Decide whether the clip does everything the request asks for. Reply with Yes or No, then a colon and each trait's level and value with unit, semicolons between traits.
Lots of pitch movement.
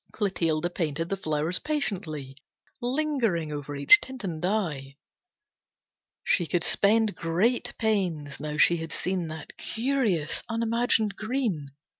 Yes: wide, 6.4 semitones